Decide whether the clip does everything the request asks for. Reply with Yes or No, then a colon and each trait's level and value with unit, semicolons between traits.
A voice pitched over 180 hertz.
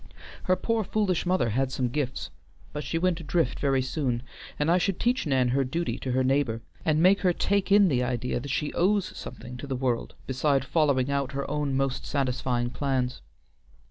No: medium, 140 Hz